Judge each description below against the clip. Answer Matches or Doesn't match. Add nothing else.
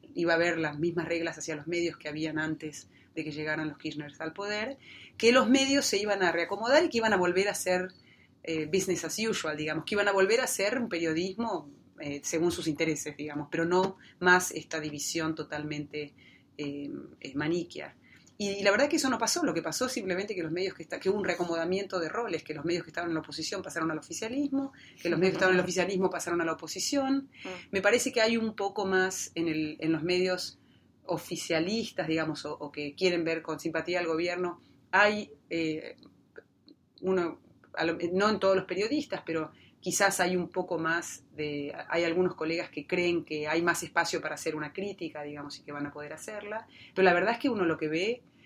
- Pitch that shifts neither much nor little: Matches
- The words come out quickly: Matches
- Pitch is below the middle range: Doesn't match